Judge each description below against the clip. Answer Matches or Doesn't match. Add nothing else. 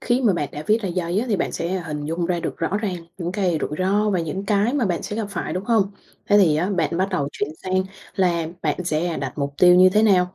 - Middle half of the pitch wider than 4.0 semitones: Doesn't match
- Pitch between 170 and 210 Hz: Matches